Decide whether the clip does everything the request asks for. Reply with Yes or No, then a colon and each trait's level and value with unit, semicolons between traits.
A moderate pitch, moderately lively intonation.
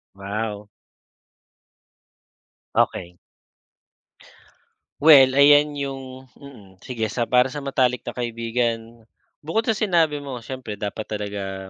No: low, 125 Hz; average, 4.7 semitones